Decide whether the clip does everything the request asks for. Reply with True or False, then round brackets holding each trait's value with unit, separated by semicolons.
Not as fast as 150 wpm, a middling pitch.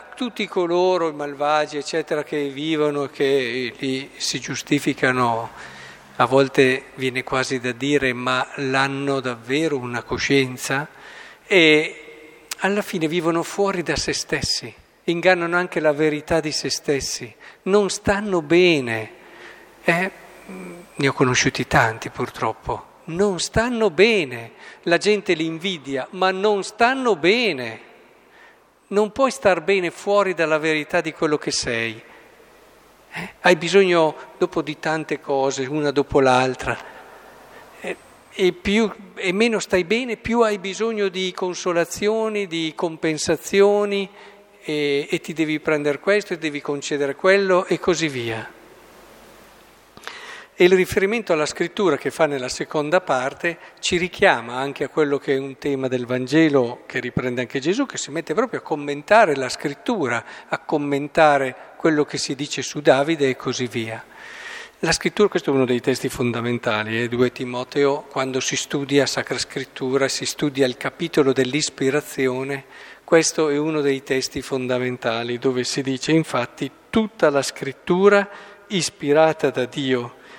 True (140 wpm; 150 Hz)